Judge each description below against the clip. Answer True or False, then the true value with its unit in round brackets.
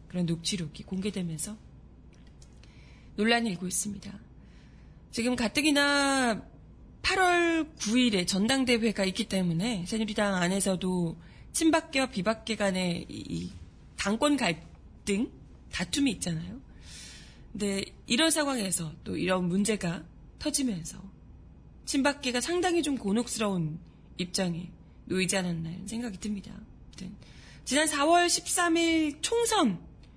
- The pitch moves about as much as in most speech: False (6.8 semitones)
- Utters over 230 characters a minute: True (245 characters per minute)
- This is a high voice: True (210 Hz)